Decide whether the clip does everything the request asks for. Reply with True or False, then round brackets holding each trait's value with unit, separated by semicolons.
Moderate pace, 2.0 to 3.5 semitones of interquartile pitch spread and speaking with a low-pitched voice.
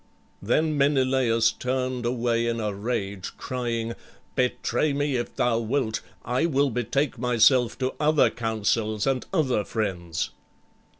False (125 wpm; 2.8 semitones; 120 Hz)